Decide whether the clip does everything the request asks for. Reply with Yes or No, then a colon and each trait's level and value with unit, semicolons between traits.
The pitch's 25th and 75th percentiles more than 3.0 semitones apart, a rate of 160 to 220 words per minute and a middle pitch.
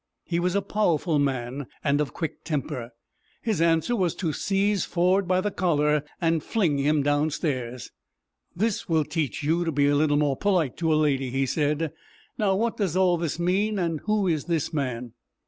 Yes: average, 4.2 semitones; average, 180 wpm; medium, 160 Hz